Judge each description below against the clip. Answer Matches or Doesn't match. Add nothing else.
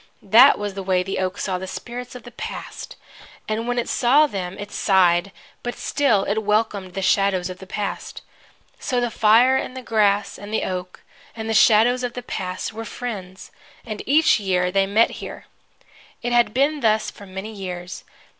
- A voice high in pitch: Matches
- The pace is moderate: Matches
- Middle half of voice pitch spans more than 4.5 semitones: Doesn't match